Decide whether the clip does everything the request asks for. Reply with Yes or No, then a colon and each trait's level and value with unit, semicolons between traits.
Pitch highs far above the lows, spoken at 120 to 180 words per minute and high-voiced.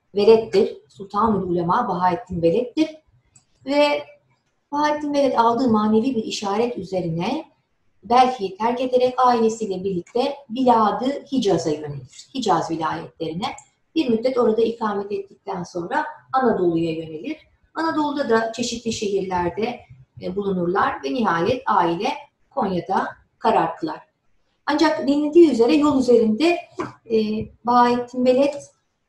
No: wide, 6.1 semitones; average, 100 wpm; high, 230 Hz